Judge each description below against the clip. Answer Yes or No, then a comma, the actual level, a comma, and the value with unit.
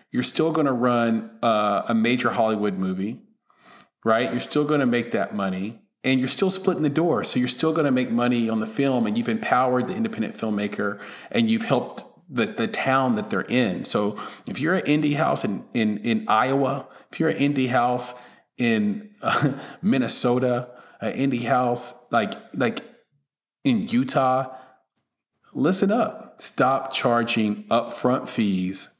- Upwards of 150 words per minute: Yes, average, 160 wpm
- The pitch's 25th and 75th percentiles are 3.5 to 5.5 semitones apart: Yes, average, 4.5 semitones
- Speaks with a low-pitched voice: Yes, low, 130 Hz